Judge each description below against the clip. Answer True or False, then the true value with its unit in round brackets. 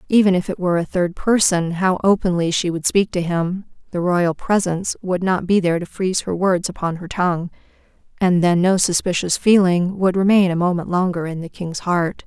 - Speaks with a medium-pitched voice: True (180 Hz)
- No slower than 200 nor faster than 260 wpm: True (205 wpm)